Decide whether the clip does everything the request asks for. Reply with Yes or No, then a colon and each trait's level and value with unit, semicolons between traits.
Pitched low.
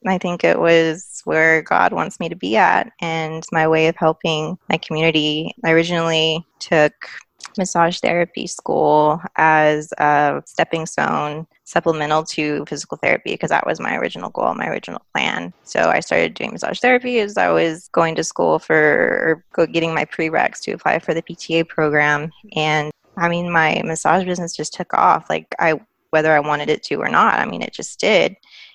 No: medium, 160 Hz